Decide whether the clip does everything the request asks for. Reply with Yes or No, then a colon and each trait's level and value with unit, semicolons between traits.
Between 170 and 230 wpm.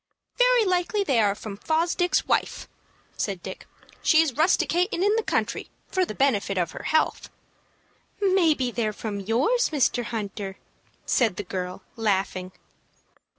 No: slow, 135 wpm